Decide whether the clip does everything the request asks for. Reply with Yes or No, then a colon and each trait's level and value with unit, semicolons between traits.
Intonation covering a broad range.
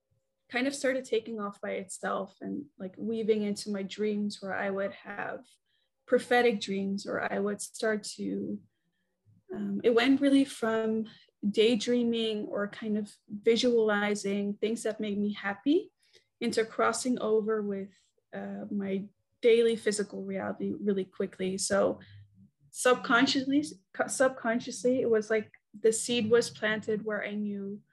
No: average, 2.8 semitones